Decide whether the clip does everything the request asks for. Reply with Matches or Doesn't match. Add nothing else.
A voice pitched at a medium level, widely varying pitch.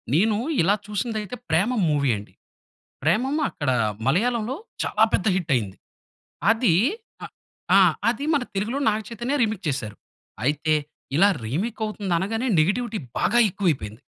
Doesn't match